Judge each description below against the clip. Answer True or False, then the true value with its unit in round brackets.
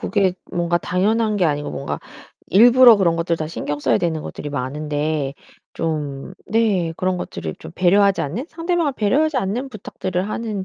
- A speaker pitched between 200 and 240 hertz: False (185 Hz)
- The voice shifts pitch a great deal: True (5.9 semitones)